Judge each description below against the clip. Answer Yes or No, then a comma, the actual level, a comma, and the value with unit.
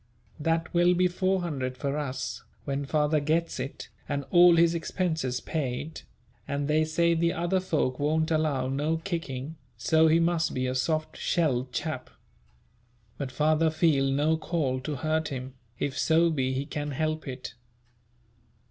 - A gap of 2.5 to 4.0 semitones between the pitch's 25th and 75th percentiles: Yes, average, 3.2 semitones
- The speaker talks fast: No, average, 155 wpm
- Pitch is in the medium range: Yes, medium, 155 Hz